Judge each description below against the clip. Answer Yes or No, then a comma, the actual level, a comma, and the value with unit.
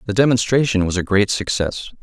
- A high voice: No, low, 105 Hz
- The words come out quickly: No, average, 180 wpm